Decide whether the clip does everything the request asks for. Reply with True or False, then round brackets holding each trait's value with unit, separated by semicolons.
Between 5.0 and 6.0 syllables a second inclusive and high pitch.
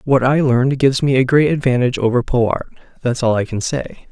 False (5.9 syllables/s; 130 Hz)